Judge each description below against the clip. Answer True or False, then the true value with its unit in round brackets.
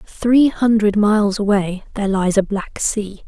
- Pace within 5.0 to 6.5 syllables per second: False (4.3 syllables/s)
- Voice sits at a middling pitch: False (205 Hz)